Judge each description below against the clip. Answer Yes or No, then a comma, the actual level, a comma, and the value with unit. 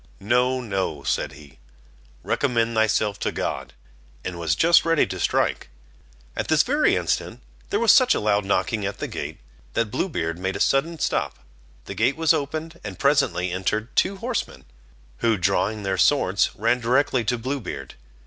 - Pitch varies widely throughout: Yes, wide, 6.9 semitones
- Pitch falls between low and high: No, low, 110 Hz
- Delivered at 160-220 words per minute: Yes, average, 170 wpm